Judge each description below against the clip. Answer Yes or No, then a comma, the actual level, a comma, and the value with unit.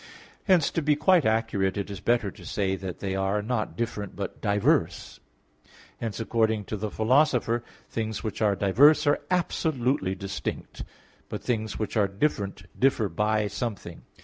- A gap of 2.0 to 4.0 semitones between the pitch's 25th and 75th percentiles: Yes, average, 3.7 semitones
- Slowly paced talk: No, average, 165 wpm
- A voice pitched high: No, low, 110 Hz